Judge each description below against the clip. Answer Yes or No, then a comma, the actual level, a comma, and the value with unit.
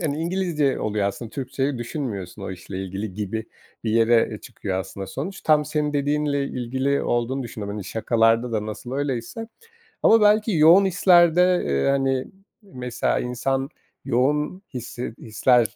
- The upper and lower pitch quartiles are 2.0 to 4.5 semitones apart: No, average, 5.2 semitones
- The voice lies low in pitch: Yes, low, 130 Hz